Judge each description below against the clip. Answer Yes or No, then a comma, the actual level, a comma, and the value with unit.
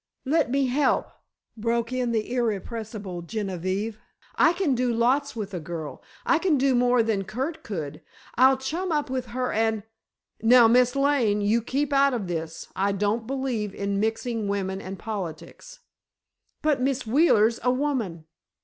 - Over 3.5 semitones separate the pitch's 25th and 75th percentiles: Yes, average, 4.5 semitones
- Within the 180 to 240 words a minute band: No, average, 160 wpm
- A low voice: No, high, 235 Hz